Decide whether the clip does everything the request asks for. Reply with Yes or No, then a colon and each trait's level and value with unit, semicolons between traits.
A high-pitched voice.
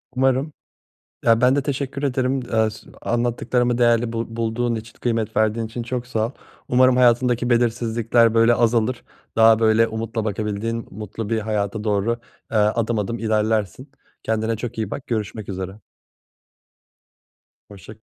No: low, 115 Hz